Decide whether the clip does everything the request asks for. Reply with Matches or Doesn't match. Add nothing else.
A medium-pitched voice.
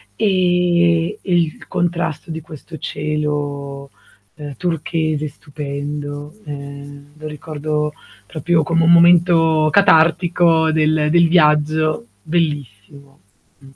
Matches